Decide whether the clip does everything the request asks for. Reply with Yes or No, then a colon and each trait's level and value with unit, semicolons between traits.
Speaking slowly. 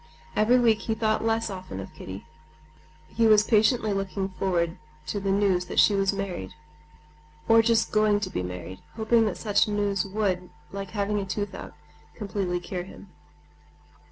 No: average, 165 wpm